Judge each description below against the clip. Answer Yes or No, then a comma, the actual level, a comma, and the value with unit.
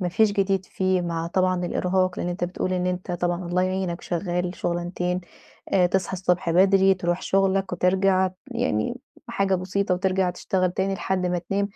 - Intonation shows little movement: Yes, narrow, 1.3 semitones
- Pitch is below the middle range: No, medium, 185 Hz